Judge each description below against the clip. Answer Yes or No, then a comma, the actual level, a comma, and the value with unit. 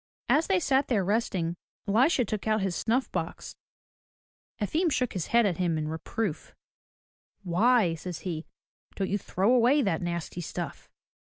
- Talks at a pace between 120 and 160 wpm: Yes, average, 155 wpm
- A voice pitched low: No, high, 200 Hz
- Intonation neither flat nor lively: No, wide, 5.9 semitones